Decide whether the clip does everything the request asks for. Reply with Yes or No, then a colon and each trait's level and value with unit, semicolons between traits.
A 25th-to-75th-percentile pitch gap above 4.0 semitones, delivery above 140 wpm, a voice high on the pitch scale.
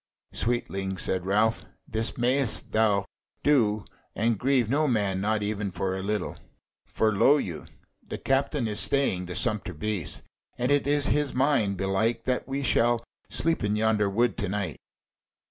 No: average, 4.4 semitones; average, 160 wpm; low, 110 Hz